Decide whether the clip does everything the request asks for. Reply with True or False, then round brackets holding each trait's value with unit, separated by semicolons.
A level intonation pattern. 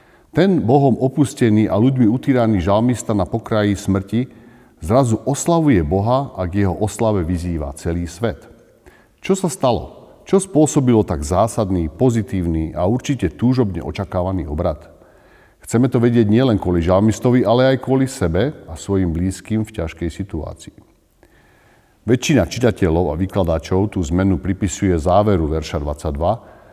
False (5.4 semitones)